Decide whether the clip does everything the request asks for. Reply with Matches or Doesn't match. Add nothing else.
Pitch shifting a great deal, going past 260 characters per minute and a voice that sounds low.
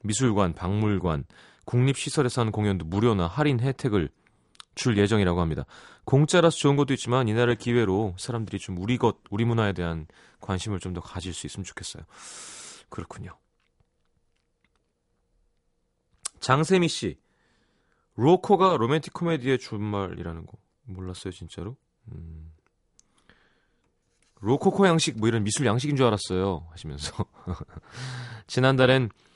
Matches